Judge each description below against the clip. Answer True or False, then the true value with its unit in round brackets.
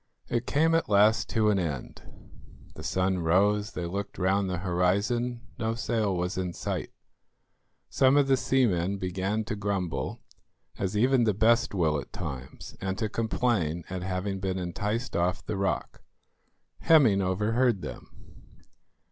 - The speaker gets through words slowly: False (150 wpm)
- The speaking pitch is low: True (100 Hz)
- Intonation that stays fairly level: False (3.7 semitones)